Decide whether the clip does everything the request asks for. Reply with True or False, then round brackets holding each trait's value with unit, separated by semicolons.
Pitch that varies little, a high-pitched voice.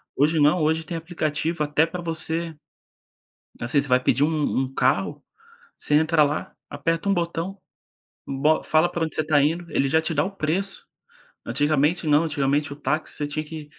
False (2.1 semitones; 155 Hz)